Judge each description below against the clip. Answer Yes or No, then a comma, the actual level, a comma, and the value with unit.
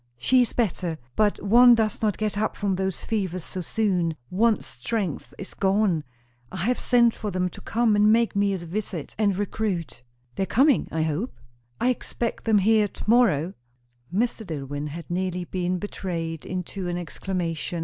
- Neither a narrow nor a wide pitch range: Yes, average, 3.9 semitones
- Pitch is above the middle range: Yes, high, 195 Hz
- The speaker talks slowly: No, average, 175 wpm